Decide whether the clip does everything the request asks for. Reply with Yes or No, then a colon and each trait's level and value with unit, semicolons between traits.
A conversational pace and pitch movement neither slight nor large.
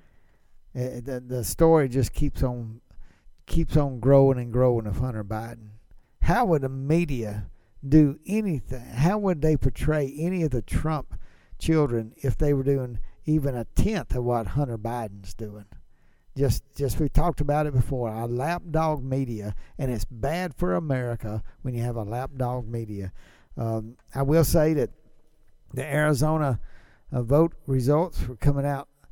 Yes: average, 155 wpm; average, 4.8 semitones